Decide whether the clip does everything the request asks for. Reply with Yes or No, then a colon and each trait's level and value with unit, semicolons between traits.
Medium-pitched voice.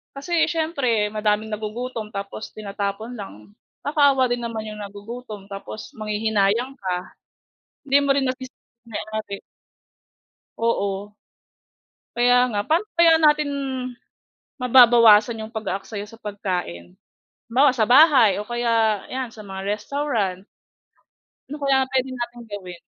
No: high, 225 Hz